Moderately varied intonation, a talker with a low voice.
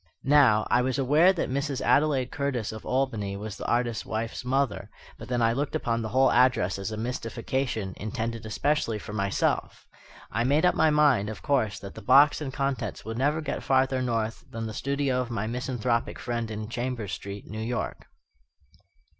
Yes: average, 3.7 semitones; low, 120 Hz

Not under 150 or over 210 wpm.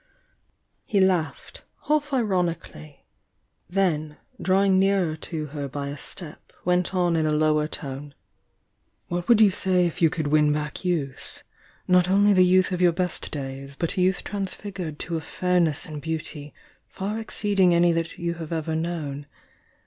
Yes: average, 165 wpm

